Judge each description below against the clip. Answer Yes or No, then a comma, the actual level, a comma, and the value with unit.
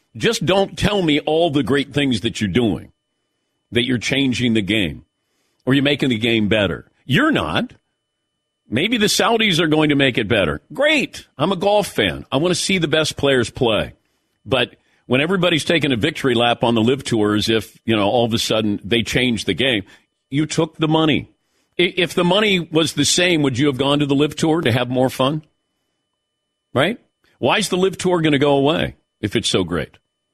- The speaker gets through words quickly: Yes, fast, 210 wpm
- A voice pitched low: No, medium, 145 Hz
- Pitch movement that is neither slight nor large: No, wide, 5.9 semitones